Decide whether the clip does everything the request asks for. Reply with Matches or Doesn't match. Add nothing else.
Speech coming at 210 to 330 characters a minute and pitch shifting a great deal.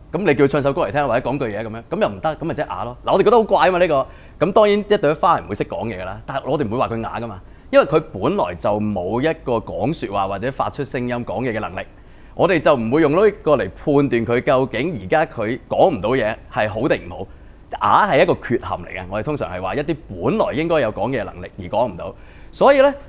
Doesn't match